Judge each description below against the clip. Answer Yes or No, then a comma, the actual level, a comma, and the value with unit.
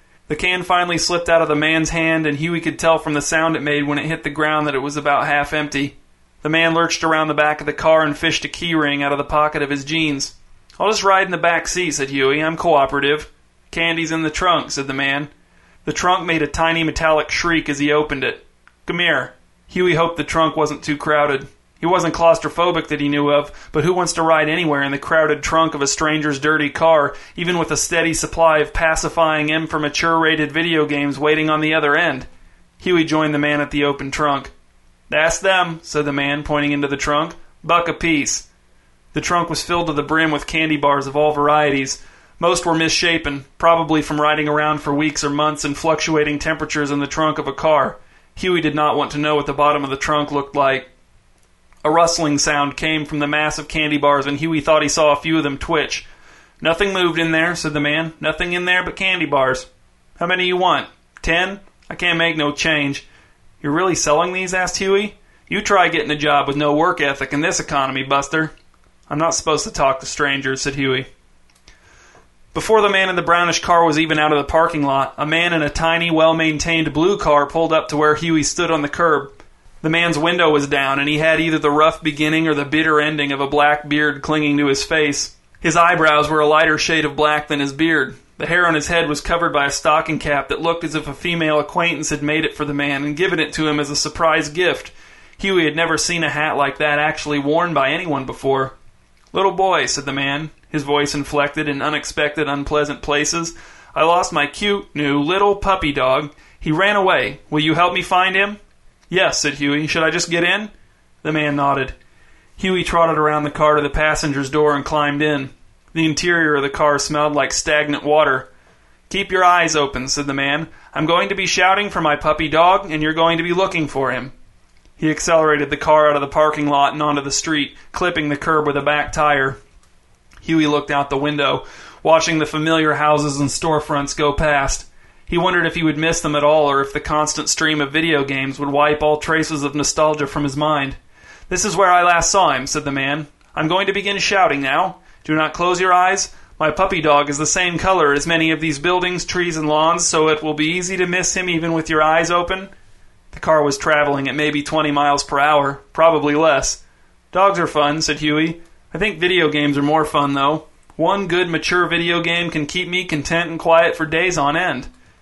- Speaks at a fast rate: Yes, fast, 220 wpm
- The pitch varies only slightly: Yes, narrow, 2.2 semitones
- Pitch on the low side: No, medium, 155 Hz